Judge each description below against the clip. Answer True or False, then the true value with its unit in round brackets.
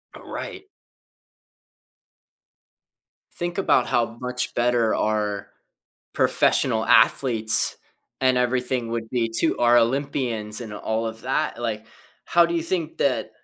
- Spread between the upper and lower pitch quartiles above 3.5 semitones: False (2.8 semitones)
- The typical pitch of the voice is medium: False (120 Hz)